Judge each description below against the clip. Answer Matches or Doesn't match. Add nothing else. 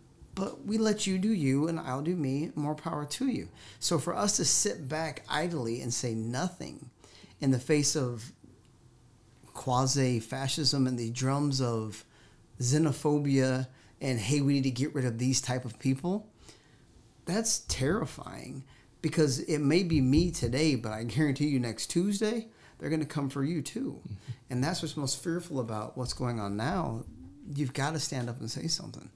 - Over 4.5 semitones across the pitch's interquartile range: Doesn't match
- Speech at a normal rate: Matches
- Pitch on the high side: Doesn't match